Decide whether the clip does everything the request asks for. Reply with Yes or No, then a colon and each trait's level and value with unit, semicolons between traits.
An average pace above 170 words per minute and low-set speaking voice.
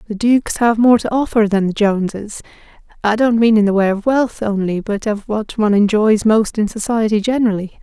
No: average, 200 wpm; high, 215 Hz